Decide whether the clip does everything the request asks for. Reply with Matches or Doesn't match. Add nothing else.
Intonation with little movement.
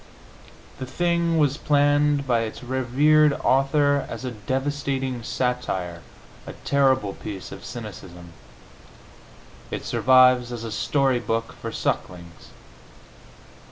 Doesn't match